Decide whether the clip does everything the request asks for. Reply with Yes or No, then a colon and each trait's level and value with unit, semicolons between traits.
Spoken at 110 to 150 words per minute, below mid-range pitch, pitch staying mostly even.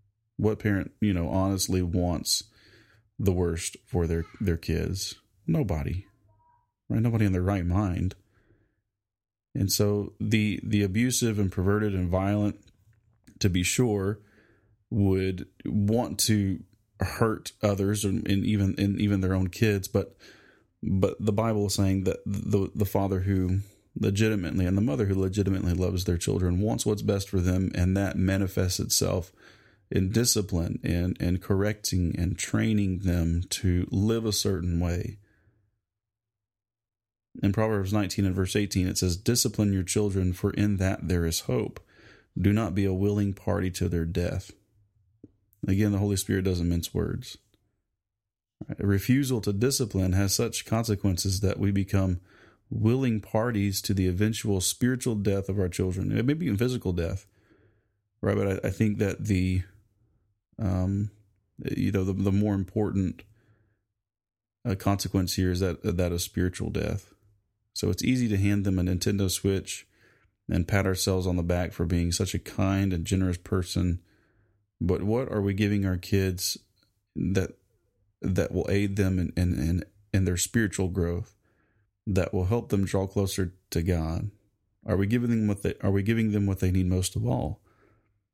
No: average, 160 wpm; low, 100 Hz; narrow, 2.1 semitones